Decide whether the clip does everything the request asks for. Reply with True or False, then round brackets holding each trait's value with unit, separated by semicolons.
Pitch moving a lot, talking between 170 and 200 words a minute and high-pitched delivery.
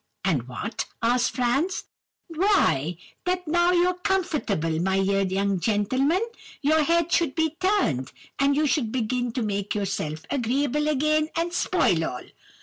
False (8.9 semitones; 145 wpm; 260 Hz)